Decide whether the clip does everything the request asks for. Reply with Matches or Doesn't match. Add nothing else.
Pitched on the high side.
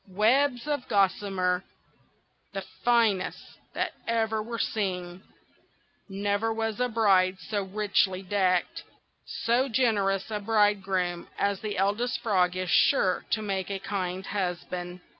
Matches